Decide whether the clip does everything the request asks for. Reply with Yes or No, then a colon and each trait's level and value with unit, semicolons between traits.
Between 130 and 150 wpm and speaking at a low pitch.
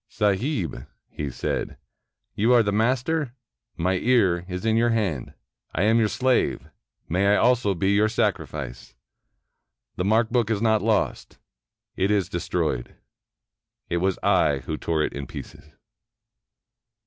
Yes: average, 140 wpm; low, 100 Hz